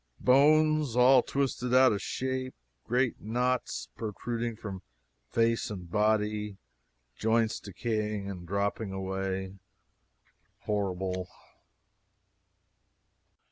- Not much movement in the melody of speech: No, average, 4.2 semitones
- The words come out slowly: Yes, slow, 85 wpm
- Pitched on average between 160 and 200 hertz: No, low, 110 Hz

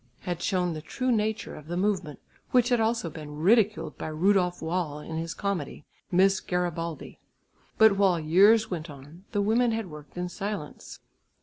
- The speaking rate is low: No, average, 170 wpm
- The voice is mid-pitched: Yes, medium, 180 Hz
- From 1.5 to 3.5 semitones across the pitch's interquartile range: No, average, 4.5 semitones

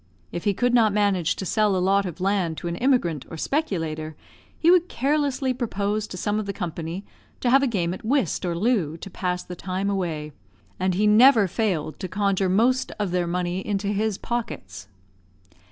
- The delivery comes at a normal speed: Yes, average, 195 wpm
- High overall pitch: Yes, high, 195 Hz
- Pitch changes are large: No, average, 4.0 semitones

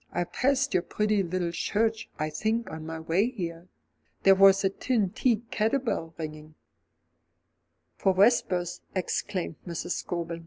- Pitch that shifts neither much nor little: Yes, average, 4.5 semitones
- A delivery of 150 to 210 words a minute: Yes, average, 155 wpm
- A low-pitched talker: No, medium, 185 Hz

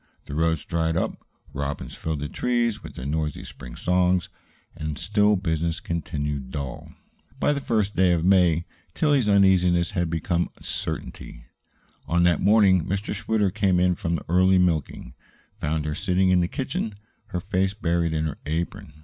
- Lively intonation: No, average, 3.4 semitones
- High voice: No, very low, 85 Hz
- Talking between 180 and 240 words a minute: No, average, 165 wpm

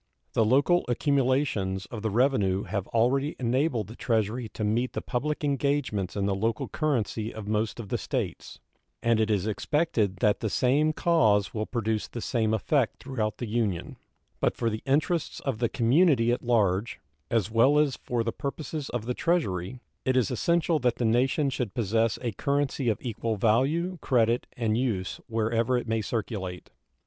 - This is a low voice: Yes, low, 115 Hz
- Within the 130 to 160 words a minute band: No, average, 175 wpm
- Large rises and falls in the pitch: No, average, 3.8 semitones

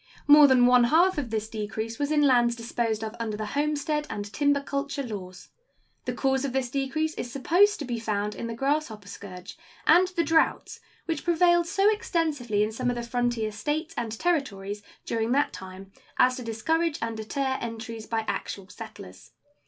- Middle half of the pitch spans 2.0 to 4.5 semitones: No, average, 5.2 semitones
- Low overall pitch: No, high, 245 Hz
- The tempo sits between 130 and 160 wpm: No, average, 185 wpm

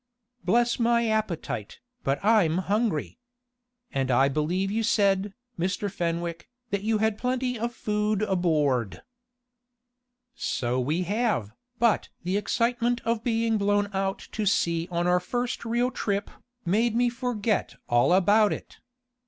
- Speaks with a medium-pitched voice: No, high, 205 Hz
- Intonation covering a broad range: No, average, 4.9 semitones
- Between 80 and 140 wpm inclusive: Yes, slow, 135 wpm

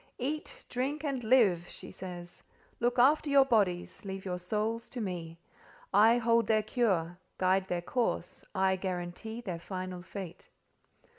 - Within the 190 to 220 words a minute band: No, average, 140 wpm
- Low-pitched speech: No, high, 200 Hz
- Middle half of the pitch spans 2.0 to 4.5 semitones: No, average, 5.1 semitones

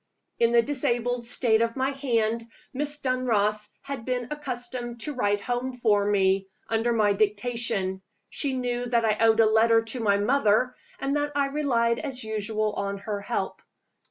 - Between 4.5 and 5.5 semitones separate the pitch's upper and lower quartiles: No, average, 3.0 semitones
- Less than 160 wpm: No, average, 165 wpm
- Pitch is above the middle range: Yes, high, 235 Hz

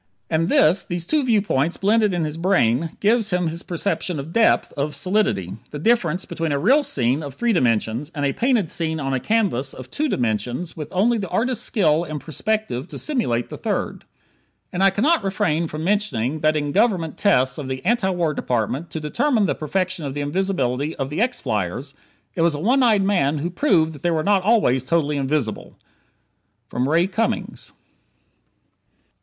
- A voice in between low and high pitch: Yes, medium, 165 Hz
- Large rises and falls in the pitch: Yes, wide, 6.2 semitones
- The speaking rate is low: No, average, 185 wpm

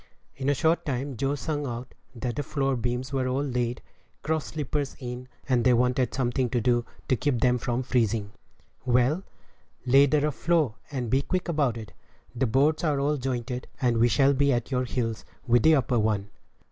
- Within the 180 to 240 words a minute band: Yes, average, 195 wpm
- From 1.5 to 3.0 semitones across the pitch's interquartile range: Yes, average, 2.7 semitones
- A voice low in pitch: Yes, low, 130 Hz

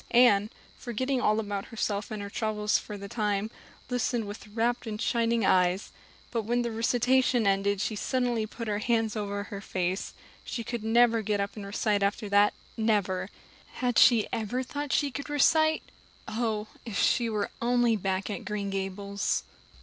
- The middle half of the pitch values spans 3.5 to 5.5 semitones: No, average, 2.9 semitones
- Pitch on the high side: Yes, high, 215 Hz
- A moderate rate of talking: Yes, average, 170 wpm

